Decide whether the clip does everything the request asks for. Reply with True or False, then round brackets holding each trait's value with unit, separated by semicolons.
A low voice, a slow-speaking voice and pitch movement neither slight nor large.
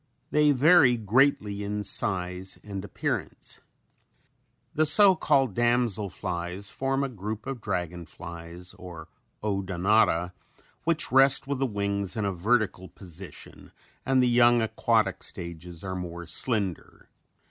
False (100 Hz; 125 wpm; 5.7 semitones)